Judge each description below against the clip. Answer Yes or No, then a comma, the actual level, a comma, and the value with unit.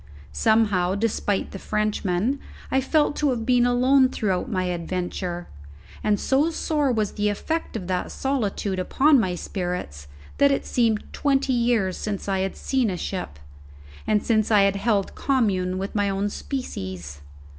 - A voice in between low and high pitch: No, high, 210 Hz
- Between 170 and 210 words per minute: No, average, 155 wpm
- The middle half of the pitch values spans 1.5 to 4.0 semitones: No, average, 5.3 semitones